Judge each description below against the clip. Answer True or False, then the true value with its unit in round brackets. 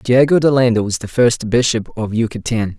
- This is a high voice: False (115 Hz)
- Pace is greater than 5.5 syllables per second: False (5.1 syllables/s)